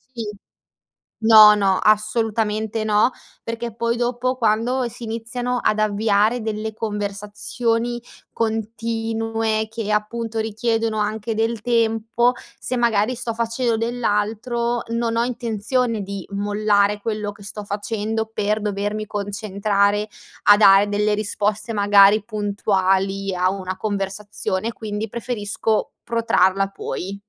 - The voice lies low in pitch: No, high, 215 Hz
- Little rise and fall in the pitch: Yes, narrow, 1.9 semitones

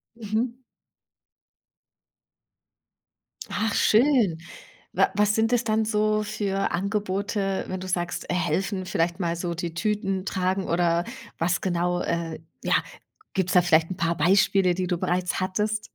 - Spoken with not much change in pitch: No, average, 3.2 semitones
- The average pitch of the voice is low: No, high, 190 Hz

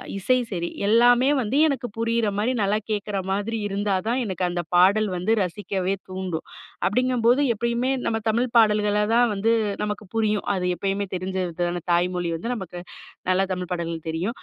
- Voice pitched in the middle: No, high, 205 Hz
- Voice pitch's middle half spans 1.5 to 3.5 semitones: No, average, 4.0 semitones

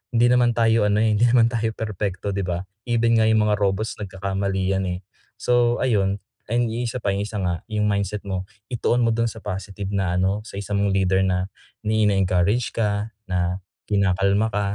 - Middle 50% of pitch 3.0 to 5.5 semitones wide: No, narrow, 2.6 semitones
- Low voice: Yes, low, 105 Hz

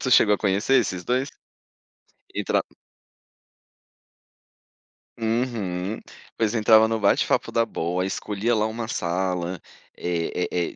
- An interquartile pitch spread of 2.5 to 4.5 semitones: Yes, average, 4.0 semitones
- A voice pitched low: Yes, low, 105 Hz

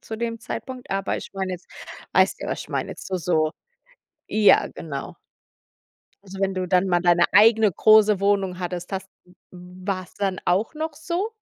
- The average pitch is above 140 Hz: Yes, high, 190 Hz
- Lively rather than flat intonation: No, average, 3.1 semitones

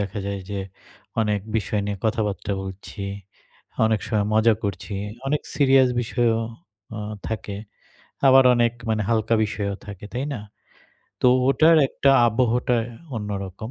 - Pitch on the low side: Yes, low, 110 Hz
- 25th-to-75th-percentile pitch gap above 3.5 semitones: No, average, 2.9 semitones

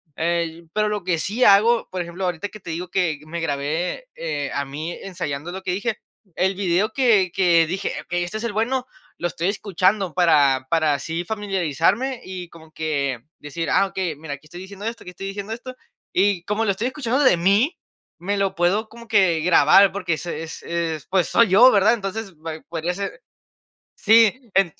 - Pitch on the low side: No, medium, 185 Hz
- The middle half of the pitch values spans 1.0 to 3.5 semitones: No, average, 3.9 semitones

